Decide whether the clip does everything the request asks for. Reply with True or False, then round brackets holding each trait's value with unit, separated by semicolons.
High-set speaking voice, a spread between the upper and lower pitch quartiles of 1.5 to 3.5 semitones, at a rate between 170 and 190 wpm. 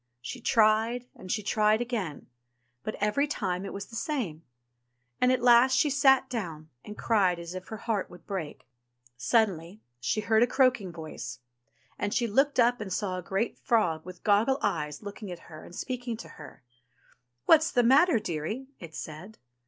False (215 Hz; 5.4 semitones; 180 wpm)